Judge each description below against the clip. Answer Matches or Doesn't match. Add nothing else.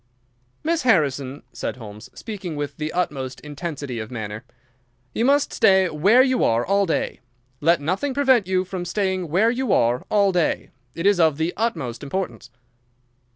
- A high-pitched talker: Doesn't match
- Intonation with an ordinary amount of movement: Doesn't match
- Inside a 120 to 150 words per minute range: Doesn't match